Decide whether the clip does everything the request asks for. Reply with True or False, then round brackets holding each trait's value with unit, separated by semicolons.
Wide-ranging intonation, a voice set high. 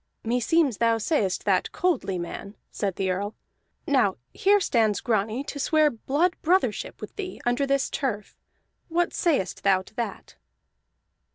True (7.4 semitones; 240 Hz)